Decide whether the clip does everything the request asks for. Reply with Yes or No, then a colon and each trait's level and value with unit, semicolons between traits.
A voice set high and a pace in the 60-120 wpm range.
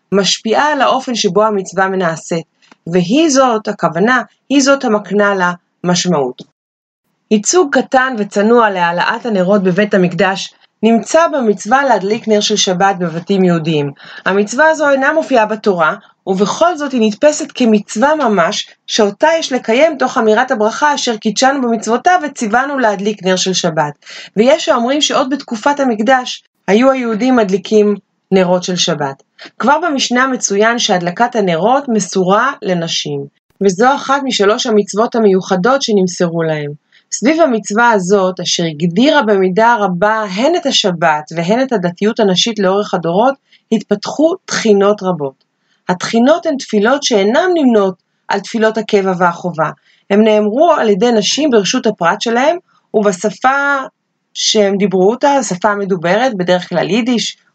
No: high, 215 Hz; average, 130 wpm